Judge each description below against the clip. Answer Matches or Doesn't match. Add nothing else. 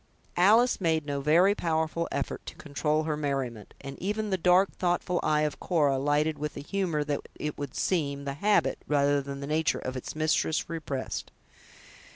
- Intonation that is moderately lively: Matches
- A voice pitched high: Doesn't match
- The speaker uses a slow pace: Doesn't match